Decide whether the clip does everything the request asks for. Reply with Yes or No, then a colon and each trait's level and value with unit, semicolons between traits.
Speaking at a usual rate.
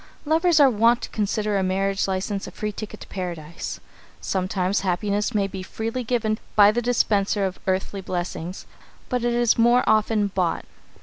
Yes: average, 170 wpm